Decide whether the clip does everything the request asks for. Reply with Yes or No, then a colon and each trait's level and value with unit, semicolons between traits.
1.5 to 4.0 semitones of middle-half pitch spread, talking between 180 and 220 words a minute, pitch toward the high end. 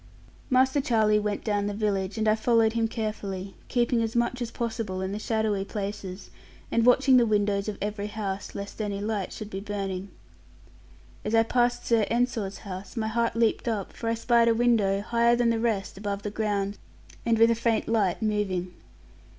Yes: narrow, 2.5 semitones; average, 190 wpm; high, 215 Hz